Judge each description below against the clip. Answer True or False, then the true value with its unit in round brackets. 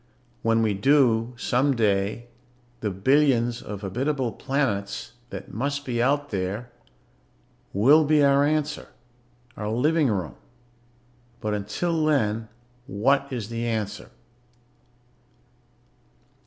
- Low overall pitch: True (120 Hz)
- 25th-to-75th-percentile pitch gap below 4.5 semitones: False (5.0 semitones)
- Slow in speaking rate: True (100 wpm)